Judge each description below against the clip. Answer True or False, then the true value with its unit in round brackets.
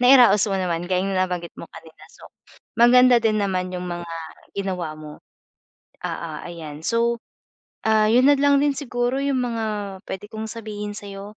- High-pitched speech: True (210 Hz)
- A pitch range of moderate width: True (4.9 semitones)